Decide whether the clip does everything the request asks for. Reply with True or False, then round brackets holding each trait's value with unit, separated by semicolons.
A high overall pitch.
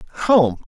True (210 Hz)